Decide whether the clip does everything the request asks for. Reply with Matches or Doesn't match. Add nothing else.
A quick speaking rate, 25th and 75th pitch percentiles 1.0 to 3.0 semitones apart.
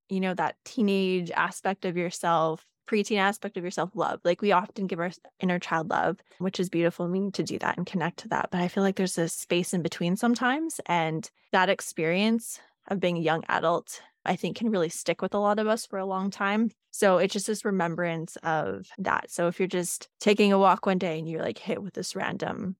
Matches